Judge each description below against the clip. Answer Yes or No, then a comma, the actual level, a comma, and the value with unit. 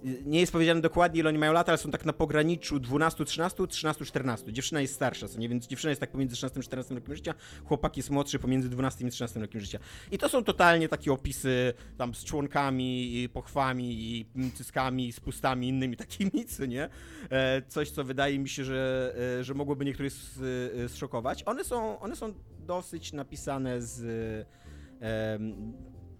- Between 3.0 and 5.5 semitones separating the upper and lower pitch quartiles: Yes, average, 3.4 semitones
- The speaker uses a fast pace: Yes, fast, 175 wpm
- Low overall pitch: Yes, low, 130 Hz